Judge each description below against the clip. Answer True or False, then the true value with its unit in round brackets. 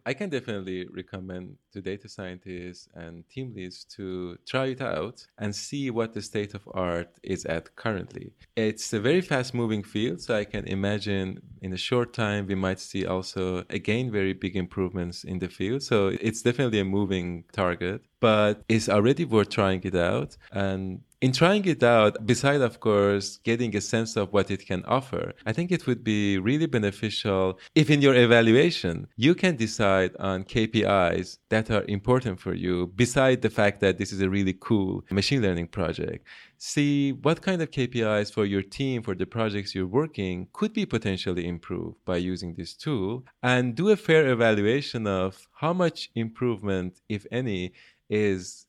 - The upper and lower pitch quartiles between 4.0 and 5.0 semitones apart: True (4.5 semitones)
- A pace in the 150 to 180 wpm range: True (175 wpm)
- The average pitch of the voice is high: False (105 Hz)